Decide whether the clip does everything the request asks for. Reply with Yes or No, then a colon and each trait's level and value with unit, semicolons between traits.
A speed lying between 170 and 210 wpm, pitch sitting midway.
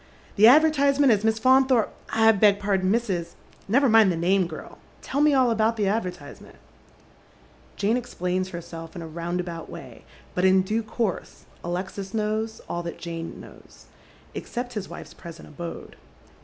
No: average, 180 wpm; high, 200 Hz